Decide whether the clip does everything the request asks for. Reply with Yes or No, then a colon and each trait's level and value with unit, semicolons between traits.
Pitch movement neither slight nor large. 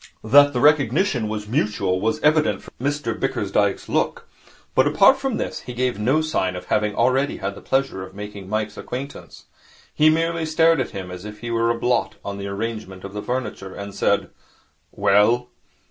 No: wide, 5.9 semitones